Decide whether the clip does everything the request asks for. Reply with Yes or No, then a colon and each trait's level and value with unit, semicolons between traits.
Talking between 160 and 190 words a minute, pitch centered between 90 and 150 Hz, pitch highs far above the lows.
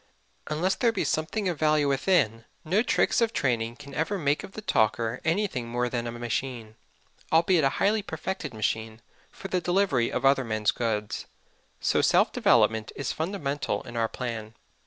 Yes: average, 170 wpm; low, 135 Hz; wide, 7.1 semitones